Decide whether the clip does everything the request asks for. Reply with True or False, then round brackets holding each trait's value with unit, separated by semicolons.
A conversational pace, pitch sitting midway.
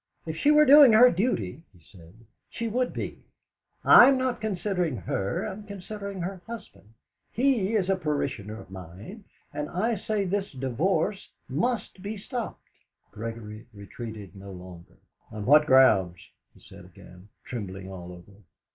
True (145 wpm; 155 Hz)